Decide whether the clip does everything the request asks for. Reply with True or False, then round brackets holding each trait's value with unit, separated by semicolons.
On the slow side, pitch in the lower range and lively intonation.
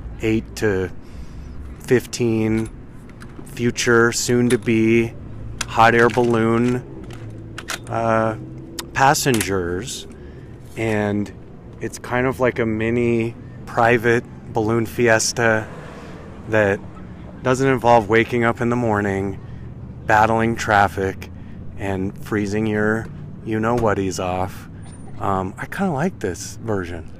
False (100 wpm; 110 Hz; 3.3 semitones)